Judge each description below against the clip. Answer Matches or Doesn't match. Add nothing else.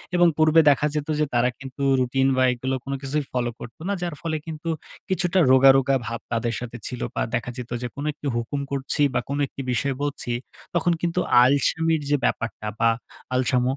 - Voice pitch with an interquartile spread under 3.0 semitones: Doesn't match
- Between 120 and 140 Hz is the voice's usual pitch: Matches